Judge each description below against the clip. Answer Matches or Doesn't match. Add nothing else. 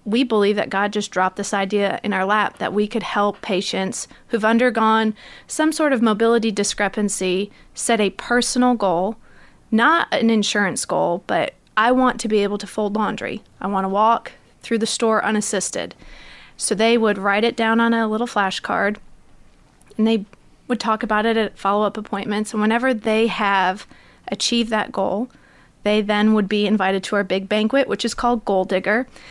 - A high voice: Matches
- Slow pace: Doesn't match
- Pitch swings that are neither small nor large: Doesn't match